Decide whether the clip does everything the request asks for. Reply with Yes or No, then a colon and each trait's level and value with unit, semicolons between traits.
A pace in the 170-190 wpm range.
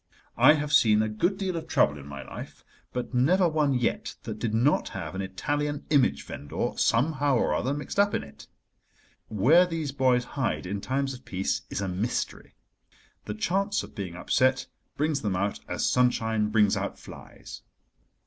Yes: average, 175 wpm